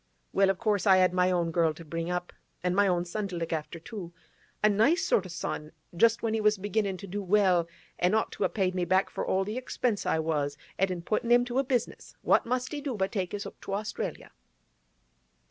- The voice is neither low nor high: No, high, 195 Hz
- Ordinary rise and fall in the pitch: Yes, average, 3.5 semitones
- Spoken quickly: Yes, fast, 240 wpm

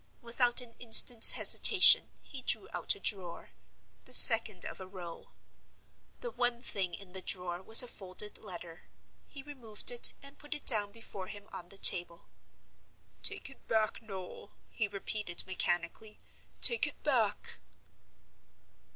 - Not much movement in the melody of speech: No, average, 4.6 semitones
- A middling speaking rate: Yes, average, 145 wpm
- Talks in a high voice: Yes, high, 210 Hz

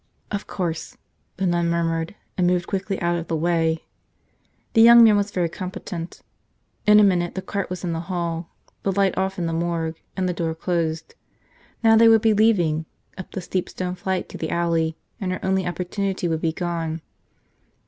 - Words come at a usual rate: Yes, average, 190 wpm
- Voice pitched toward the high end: No, medium, 175 Hz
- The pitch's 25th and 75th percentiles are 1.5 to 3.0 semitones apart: Yes, narrow, 2.5 semitones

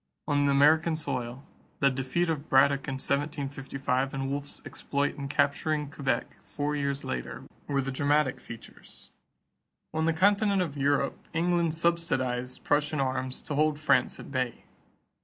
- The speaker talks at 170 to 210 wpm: No, average, 140 wpm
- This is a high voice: No, medium, 140 Hz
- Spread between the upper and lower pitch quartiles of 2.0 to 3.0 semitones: Yes, narrow, 2.5 semitones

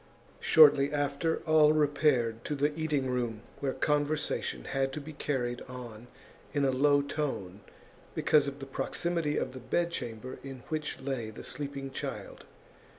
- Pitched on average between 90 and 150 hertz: Yes, medium, 140 Hz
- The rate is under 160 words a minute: Yes, average, 150 wpm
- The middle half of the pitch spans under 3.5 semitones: Yes, average, 2.7 semitones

